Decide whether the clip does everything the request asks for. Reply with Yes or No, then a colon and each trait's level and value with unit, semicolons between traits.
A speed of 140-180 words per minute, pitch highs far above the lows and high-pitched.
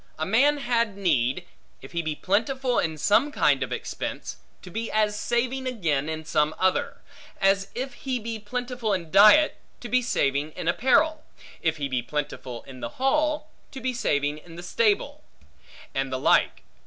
Yes: average, 175 wpm; wide, 8.5 semitones; high, 210 Hz